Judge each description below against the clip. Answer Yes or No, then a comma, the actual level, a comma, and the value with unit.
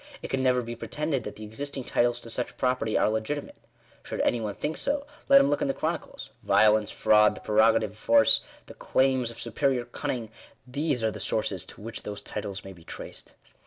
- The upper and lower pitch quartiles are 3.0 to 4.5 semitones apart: Yes, average, 3.7 semitones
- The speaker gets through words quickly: Yes, fast, 215 wpm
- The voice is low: Yes, low, 115 Hz